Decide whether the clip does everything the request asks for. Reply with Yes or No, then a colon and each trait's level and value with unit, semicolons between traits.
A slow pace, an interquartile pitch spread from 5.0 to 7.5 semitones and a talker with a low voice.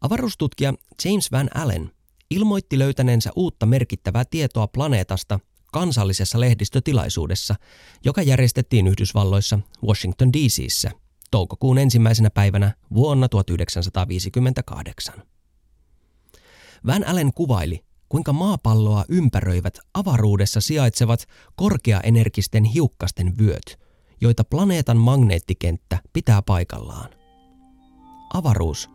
Yes: slow, 80 wpm; wide, 5.4 semitones; low, 115 Hz